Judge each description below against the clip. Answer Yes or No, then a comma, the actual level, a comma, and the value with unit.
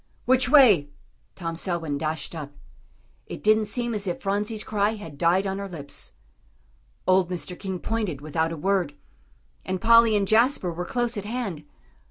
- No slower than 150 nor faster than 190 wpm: Yes, average, 165 wpm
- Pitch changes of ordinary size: Yes, average, 4.7 semitones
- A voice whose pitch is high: Yes, high, 195 Hz